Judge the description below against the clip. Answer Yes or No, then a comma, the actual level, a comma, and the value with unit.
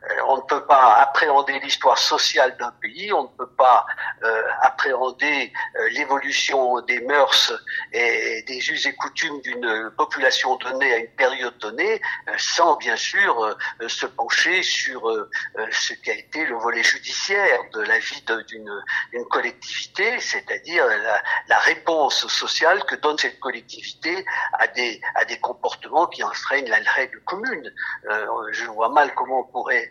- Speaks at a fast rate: No, average, 140 wpm